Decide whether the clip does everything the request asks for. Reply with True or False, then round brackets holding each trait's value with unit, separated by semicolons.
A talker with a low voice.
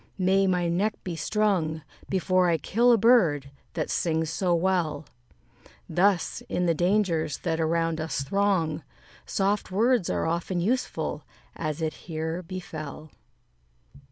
False (175 Hz)